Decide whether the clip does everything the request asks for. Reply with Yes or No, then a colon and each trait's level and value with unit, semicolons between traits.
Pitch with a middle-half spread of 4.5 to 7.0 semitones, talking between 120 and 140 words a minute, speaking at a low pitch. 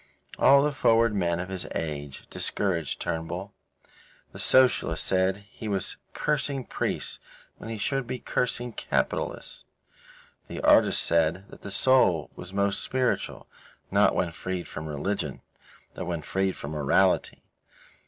Yes: wide, 5.6 semitones; slow, 135 wpm; very low, 95 Hz